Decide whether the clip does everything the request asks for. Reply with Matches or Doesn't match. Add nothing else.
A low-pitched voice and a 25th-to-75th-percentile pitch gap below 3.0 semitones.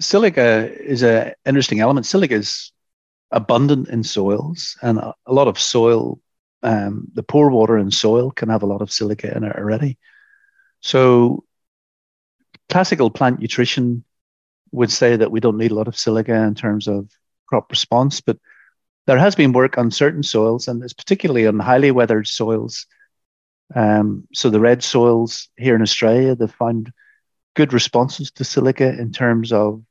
Doesn't match